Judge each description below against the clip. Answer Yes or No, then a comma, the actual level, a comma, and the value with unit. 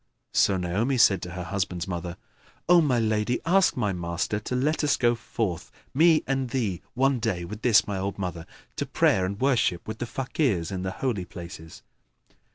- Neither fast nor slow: Yes, average, 185 wpm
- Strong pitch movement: Yes, wide, 5.9 semitones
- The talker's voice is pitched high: No, low, 105 Hz